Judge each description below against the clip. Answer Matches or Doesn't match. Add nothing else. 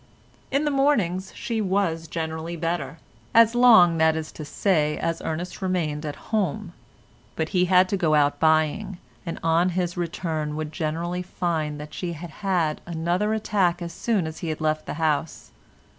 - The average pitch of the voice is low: Doesn't match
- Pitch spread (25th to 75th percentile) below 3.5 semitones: Matches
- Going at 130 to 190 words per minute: Matches